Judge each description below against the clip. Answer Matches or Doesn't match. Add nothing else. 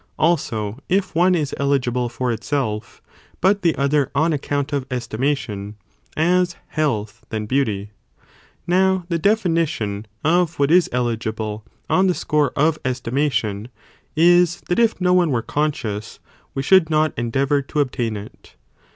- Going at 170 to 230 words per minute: Doesn't match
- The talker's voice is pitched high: Doesn't match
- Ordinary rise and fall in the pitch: Doesn't match